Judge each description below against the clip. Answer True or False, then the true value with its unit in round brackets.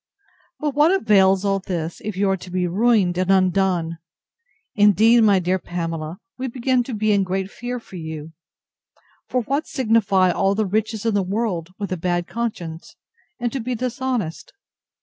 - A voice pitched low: False (195 Hz)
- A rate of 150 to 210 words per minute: True (170 wpm)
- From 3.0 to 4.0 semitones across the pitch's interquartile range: False (4.4 semitones)